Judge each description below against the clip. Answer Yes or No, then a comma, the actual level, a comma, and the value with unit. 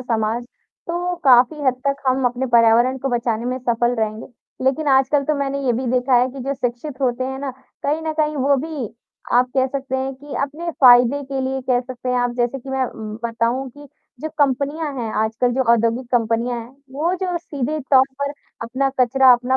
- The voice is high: Yes, very high, 260 Hz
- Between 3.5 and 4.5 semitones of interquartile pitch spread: No, narrow, 2.5 semitones